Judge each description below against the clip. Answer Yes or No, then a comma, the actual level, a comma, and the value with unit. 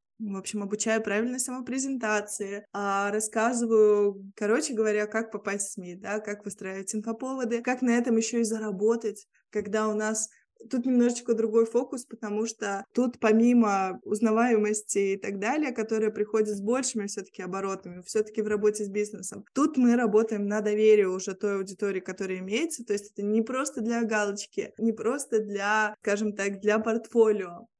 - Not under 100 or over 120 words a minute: No, average, 155 wpm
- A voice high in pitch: Yes, high, 215 Hz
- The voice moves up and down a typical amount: No, narrow, 2.1 semitones